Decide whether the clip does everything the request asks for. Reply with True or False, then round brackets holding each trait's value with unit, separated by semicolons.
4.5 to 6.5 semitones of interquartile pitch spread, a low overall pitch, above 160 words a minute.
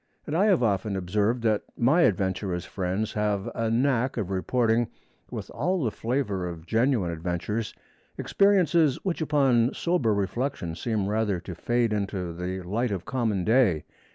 False (5.0 semitones; 110 Hz; 155 wpm)